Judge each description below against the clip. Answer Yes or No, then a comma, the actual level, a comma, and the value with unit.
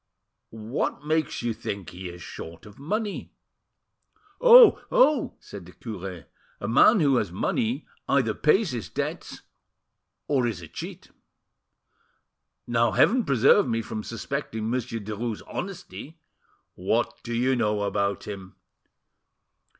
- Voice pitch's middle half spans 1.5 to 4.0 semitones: No, wide, 5.6 semitones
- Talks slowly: Yes, slow, 125 wpm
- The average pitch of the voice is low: Yes, low, 115 Hz